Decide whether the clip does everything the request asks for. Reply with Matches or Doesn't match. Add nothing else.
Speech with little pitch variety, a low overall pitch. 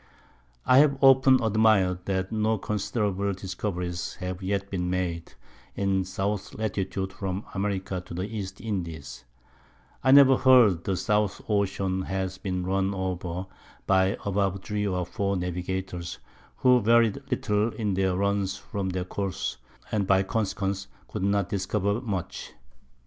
Matches